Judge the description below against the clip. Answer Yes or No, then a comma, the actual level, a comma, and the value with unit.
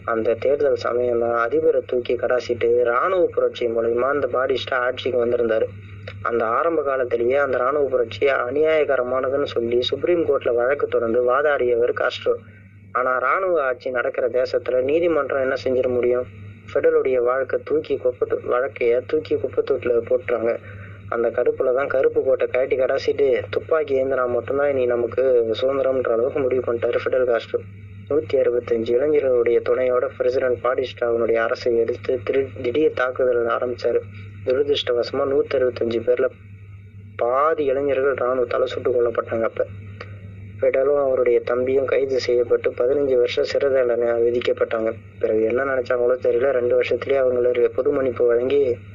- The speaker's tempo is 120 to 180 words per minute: Yes, average, 125 wpm